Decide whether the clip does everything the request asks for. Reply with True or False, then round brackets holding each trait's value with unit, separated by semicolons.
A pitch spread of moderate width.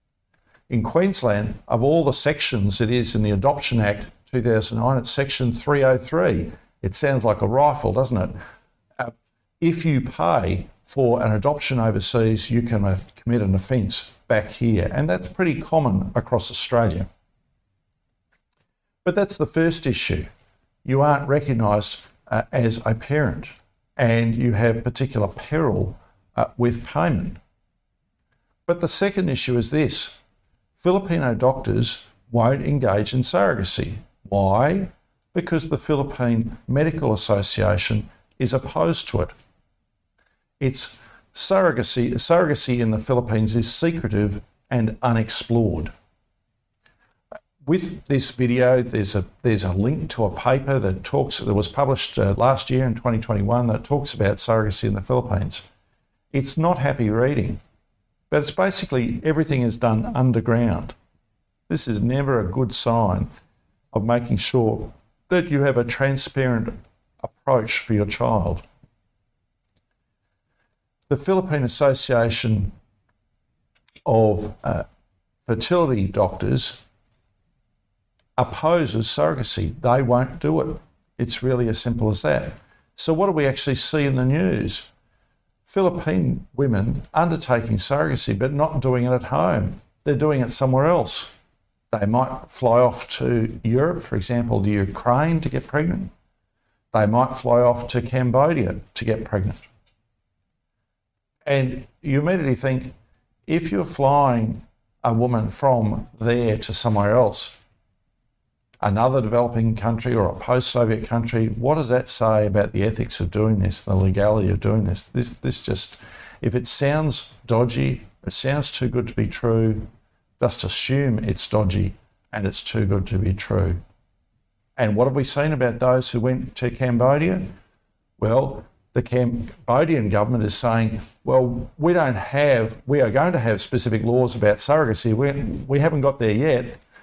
True (3.9 semitones)